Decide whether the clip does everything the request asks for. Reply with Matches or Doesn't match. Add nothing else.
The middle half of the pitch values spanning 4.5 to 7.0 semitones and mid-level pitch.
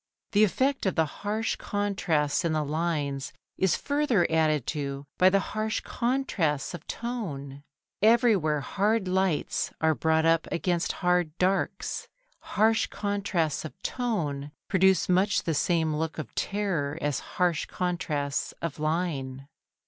Matches